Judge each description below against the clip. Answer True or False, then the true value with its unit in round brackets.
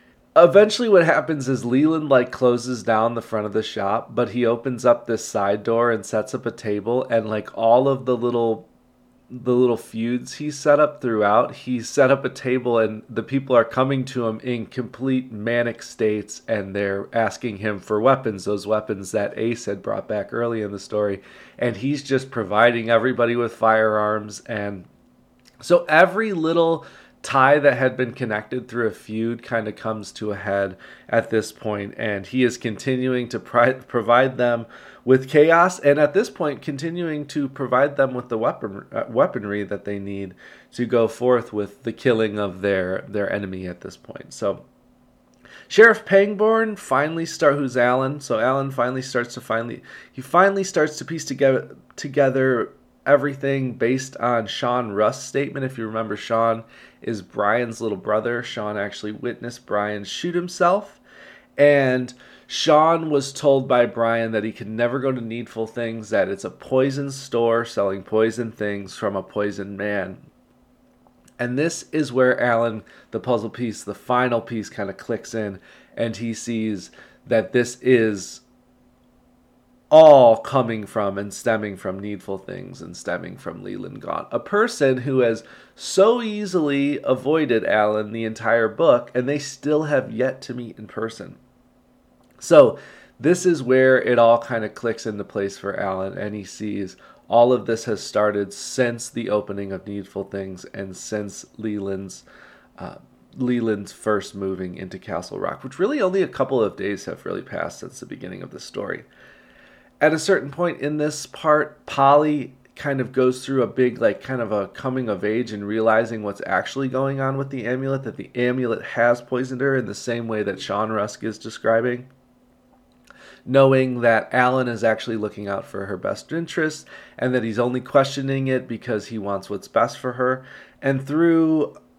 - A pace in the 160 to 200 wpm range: True (175 wpm)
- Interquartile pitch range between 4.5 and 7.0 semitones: False (3.7 semitones)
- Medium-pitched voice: False (120 Hz)